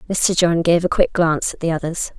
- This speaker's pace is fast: Yes, fast, 245 wpm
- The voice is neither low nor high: Yes, medium, 170 Hz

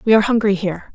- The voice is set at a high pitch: Yes, high, 205 Hz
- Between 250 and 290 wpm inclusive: Yes, fast, 255 wpm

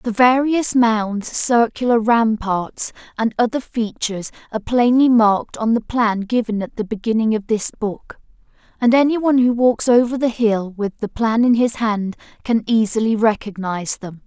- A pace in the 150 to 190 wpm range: Yes, average, 160 wpm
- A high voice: Yes, high, 225 Hz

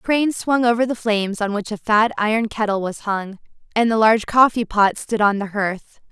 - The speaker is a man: No, female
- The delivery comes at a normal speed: No, fast, 225 wpm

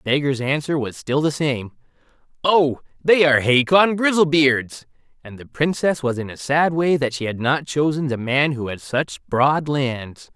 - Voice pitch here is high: No, medium, 140 Hz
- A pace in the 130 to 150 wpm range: No, average, 185 wpm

